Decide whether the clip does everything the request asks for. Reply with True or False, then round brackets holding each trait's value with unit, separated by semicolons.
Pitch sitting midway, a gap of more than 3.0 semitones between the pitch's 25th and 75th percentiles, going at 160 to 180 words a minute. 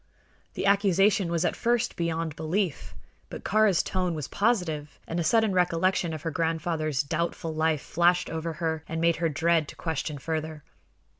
False (165 Hz; 2.4 semitones; 165 wpm)